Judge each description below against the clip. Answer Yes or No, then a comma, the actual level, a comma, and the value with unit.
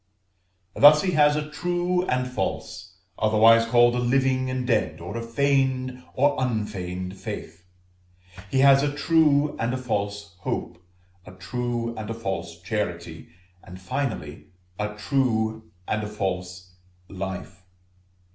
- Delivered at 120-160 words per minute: Yes, slow, 135 wpm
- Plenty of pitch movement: Yes, wide, 5.7 semitones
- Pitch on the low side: Yes, low, 115 Hz